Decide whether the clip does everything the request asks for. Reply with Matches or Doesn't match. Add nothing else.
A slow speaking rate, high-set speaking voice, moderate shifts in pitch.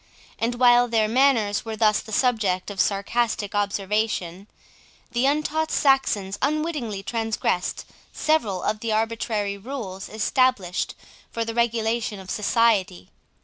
Matches